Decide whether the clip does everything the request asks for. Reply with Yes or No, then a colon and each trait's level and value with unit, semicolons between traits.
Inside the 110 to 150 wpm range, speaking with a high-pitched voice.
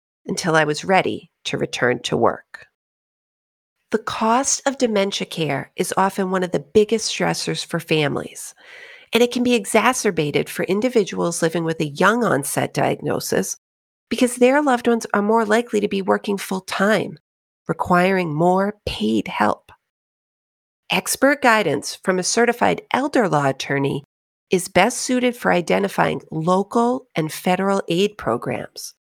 Yes: average, 140 wpm; high, 195 Hz